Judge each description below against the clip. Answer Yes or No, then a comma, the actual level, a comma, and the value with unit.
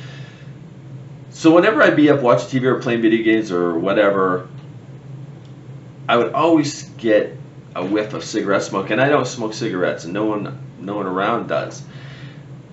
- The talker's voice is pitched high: No, low, 135 Hz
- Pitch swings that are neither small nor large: Yes, average, 4.2 semitones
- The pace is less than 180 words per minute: Yes, average, 160 wpm